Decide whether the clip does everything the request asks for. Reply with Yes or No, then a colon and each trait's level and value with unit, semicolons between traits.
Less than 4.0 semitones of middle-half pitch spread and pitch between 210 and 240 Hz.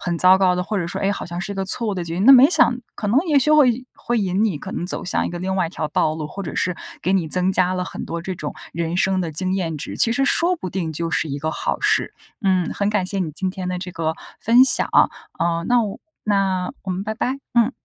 No: average, 3.5 semitones; medium, 185 Hz